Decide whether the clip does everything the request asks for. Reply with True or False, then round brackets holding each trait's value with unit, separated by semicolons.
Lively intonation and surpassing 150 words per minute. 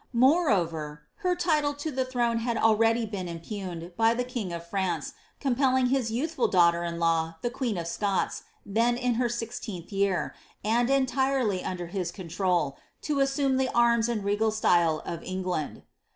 True (6.1 semitones; 165 wpm)